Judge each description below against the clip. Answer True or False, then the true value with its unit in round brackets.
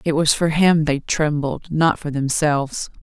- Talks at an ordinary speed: True (180 wpm)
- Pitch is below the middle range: False (150 Hz)